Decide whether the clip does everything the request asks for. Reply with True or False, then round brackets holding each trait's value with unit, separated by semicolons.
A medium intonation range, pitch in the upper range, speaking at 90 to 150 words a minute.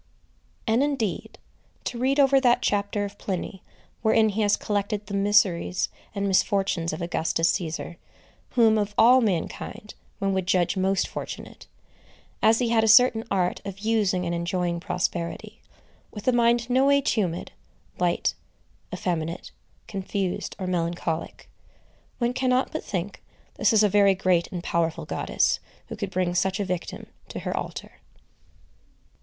True (4.0 semitones; 200 Hz; 140 wpm)